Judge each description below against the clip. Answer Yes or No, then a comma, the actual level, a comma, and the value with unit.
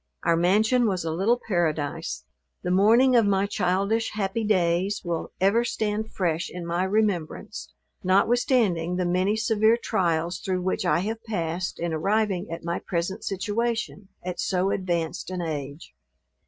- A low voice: No, high, 190 Hz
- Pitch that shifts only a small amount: No, average, 3.8 semitones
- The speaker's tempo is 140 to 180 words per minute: Yes, average, 150 wpm